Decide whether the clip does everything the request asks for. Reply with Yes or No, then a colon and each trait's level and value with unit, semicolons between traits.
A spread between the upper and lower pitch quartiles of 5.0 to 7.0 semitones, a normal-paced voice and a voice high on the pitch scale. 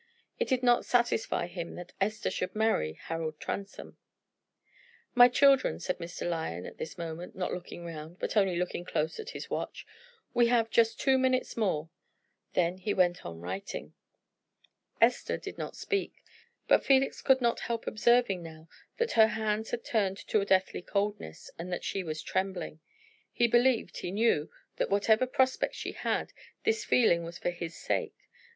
Yes: wide, 5.6 semitones; average, 170 wpm; high, 195 Hz